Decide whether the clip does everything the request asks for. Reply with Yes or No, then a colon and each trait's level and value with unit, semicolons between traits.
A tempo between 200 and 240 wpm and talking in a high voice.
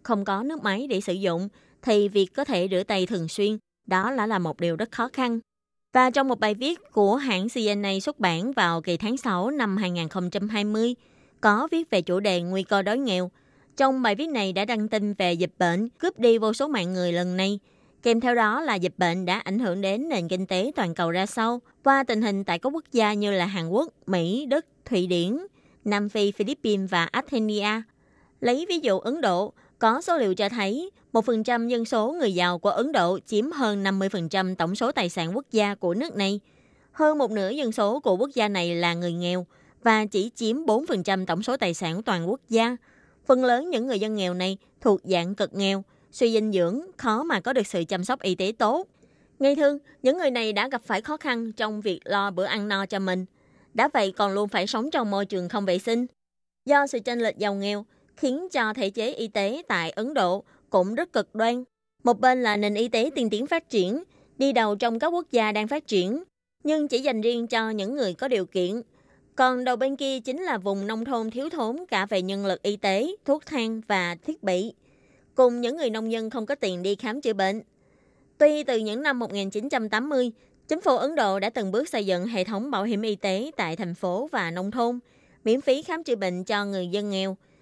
Yes: average, 225 wpm; high, 215 Hz